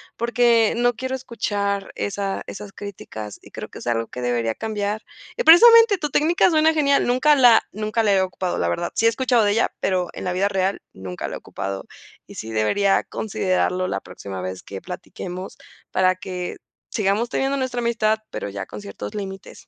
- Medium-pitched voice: No, high, 200 Hz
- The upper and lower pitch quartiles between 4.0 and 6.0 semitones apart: Yes, average, 5.1 semitones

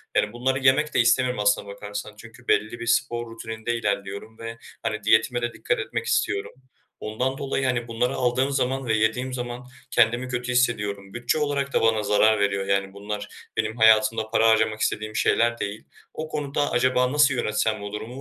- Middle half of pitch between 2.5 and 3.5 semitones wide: Yes, average, 2.8 semitones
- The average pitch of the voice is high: No, low, 115 Hz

